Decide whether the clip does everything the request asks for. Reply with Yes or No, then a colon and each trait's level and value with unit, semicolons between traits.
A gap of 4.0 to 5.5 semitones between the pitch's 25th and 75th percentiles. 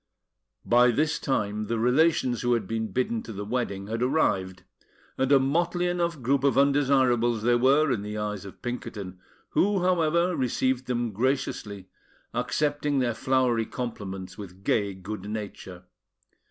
Yes: average, 4.7 semitones